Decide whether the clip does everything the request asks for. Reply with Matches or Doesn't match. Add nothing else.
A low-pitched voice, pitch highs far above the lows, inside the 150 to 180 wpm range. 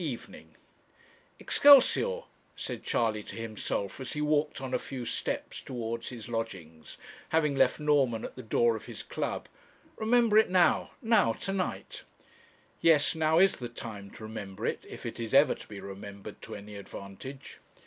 Matches